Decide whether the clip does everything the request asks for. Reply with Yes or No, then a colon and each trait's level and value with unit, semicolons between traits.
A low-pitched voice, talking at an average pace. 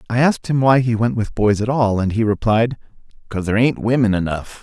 No: low, 115 Hz; fast, 235 wpm